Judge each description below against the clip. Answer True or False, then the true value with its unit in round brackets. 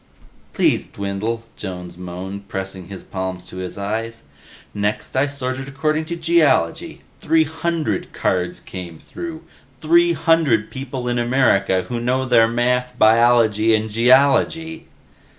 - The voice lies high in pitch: False (120 Hz)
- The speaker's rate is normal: False (130 wpm)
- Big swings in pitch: True (6.1 semitones)